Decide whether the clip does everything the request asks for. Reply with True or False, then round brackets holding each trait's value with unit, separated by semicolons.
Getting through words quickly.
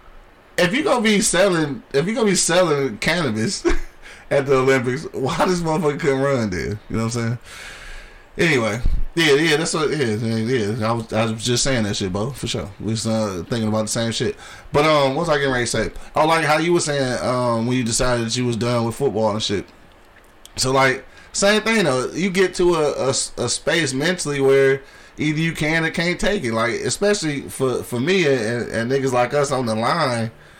True (225 wpm)